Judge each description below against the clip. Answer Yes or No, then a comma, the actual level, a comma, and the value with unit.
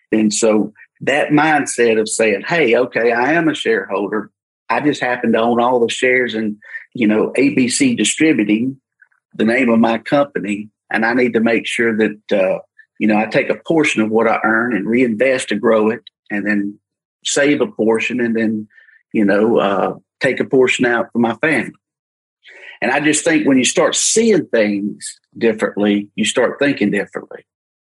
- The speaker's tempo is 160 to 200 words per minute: Yes, average, 180 wpm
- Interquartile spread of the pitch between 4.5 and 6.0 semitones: Yes, average, 4.8 semitones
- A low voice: Yes, low, 115 Hz